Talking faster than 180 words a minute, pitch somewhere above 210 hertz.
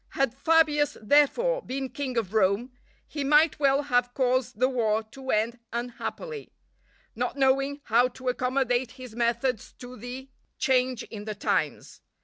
No: average, 145 wpm; very high, 255 Hz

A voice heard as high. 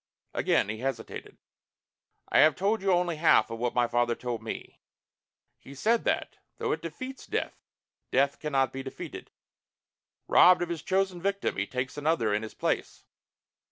No: medium, 140 Hz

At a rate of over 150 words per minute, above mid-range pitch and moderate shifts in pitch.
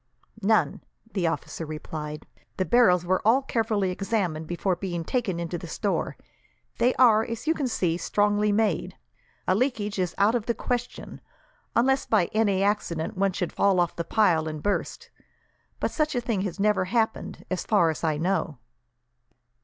Yes: average, 170 wpm; high, 195 Hz; average, 4.5 semitones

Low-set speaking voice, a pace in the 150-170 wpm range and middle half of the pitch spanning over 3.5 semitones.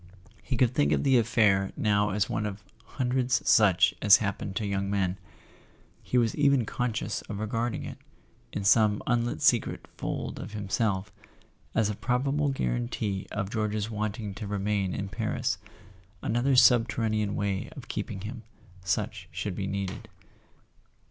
No: low, 105 Hz; average, 155 wpm; average, 2.8 semitones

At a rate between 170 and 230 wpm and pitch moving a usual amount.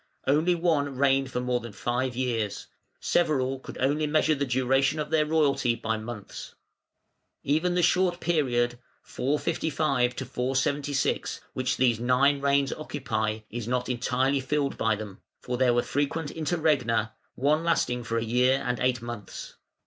No: average, 150 wpm; average, 3.4 semitones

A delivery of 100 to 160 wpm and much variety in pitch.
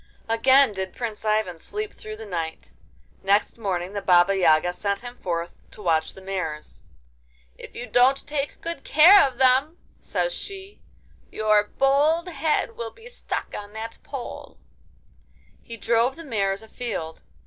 Yes: average, 150 wpm; wide, 6.2 semitones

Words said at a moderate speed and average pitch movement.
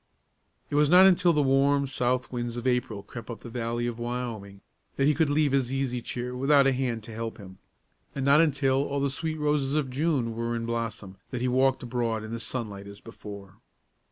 No: fast, 215 wpm; average, 3.3 semitones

